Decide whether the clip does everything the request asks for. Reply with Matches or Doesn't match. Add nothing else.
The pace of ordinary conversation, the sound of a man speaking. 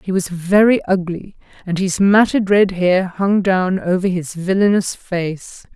Doesn't match